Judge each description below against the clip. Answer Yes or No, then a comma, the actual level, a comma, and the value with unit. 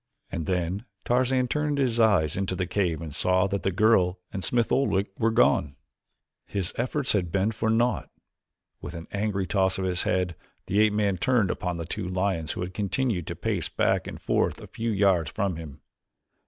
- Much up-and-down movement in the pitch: No, average, 3.8 semitones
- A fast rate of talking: No, average, 195 wpm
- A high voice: No, very low, 95 Hz